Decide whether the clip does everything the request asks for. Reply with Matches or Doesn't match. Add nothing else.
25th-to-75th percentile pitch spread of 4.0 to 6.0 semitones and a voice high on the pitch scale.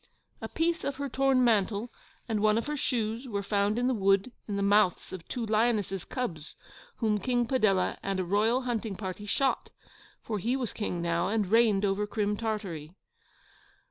Doesn't match